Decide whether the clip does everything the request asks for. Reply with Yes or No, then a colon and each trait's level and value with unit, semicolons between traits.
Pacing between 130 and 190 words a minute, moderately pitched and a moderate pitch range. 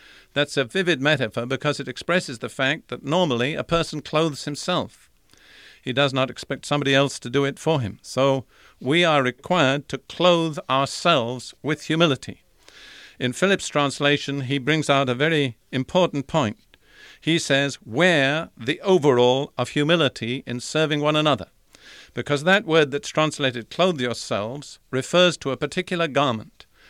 Yes: average, 150 wpm; medium, 145 Hz; average, 3.5 semitones